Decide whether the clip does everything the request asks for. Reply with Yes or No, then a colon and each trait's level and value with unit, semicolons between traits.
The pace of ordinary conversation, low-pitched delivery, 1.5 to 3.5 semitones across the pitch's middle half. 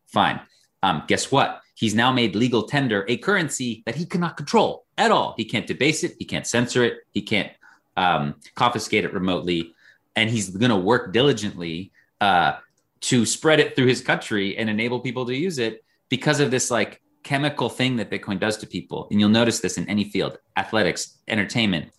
No: average, 190 wpm; low, 115 Hz; average, 4.0 semitones